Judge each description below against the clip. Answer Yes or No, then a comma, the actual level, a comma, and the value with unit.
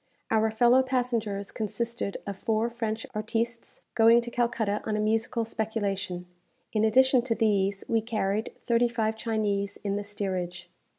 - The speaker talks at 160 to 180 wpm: No, average, 150 wpm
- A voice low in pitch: No, high, 220 Hz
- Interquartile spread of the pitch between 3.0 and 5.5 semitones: No, narrow, 2.4 semitones